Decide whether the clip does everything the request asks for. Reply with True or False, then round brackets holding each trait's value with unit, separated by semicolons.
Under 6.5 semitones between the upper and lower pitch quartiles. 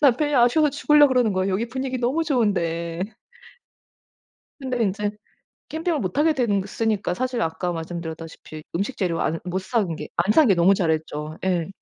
False (7.0 semitones)